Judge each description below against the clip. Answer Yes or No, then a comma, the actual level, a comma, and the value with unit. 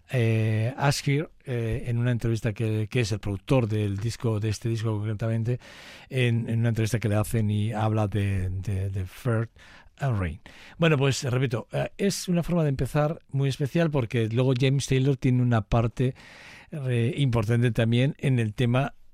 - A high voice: No, low, 120 Hz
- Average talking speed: Yes, average, 175 wpm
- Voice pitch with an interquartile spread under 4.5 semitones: Yes, average, 3.4 semitones